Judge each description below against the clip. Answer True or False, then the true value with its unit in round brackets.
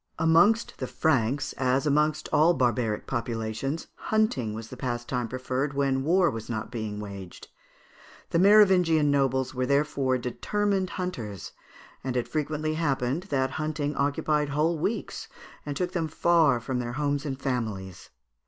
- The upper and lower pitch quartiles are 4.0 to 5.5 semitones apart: True (4.3 semitones)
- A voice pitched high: False (140 Hz)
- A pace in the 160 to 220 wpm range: False (145 wpm)